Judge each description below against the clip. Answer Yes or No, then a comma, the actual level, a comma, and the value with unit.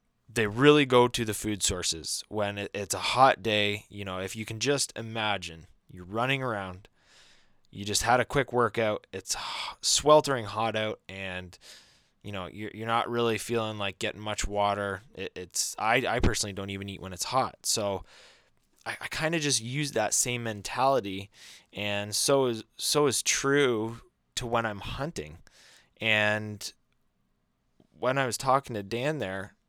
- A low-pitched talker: Yes, low, 110 Hz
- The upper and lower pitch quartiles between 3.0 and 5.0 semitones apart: Yes, average, 3.4 semitones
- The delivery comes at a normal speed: Yes, average, 170 wpm